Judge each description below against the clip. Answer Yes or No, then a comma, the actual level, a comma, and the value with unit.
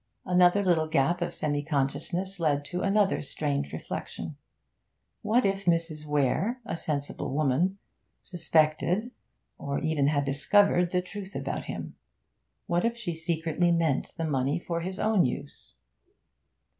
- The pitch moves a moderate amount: Yes, average, 4.1 semitones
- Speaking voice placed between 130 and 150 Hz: No, medium, 170 Hz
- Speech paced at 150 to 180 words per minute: No, slow, 135 wpm